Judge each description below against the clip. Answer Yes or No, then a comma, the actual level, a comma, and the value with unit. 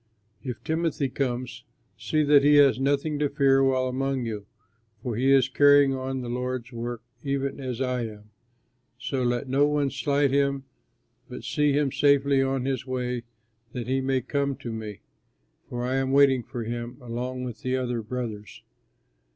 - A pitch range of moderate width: No, narrow, 2.1 semitones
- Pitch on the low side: Yes, low, 130 Hz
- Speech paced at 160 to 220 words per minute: Yes, average, 170 wpm